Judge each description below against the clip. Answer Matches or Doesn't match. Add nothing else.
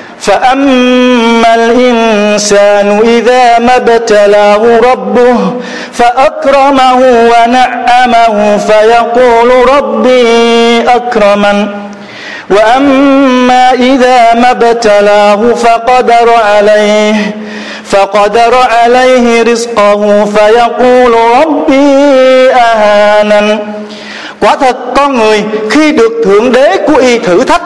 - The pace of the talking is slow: Matches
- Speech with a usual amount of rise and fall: Matches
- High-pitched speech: Matches